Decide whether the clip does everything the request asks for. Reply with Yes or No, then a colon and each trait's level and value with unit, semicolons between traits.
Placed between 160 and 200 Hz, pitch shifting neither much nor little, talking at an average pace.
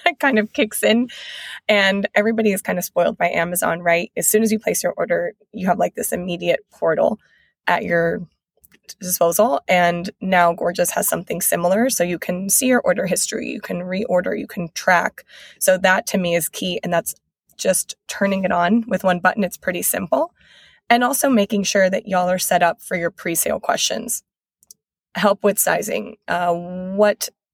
Yes: high, 190 Hz; average, 3.6 semitones; average, 185 wpm